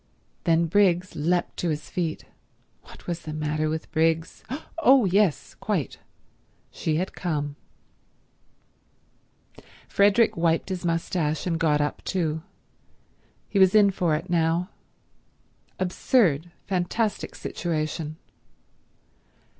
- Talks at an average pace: No, slow, 100 wpm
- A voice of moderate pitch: Yes, medium, 170 Hz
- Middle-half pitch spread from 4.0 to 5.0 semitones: No, average, 3.0 semitones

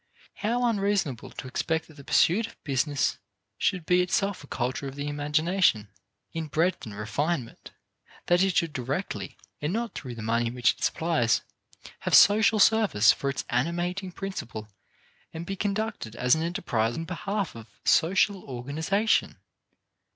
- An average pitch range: No, wide, 7.5 semitones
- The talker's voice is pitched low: No, medium, 160 Hz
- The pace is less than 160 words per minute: Yes, average, 150 wpm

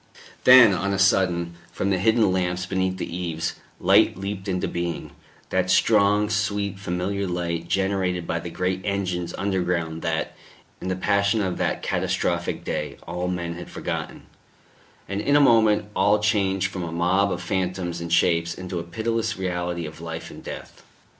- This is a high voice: No, very low, 95 Hz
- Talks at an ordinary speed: Yes, average, 165 wpm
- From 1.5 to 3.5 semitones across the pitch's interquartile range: Yes, narrow, 2.4 semitones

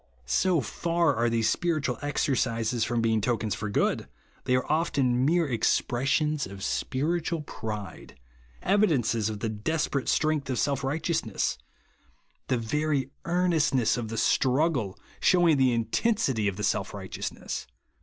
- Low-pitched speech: Yes, low, 130 Hz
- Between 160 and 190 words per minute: No, average, 140 wpm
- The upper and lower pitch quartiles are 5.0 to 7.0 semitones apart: Yes, wide, 5.6 semitones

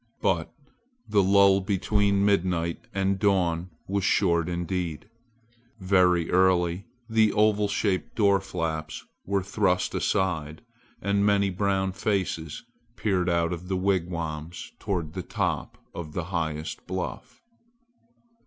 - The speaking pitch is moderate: No, very low, 95 Hz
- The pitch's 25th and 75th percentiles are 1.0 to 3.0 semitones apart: Yes, average, 2.7 semitones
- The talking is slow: Yes, slow, 115 wpm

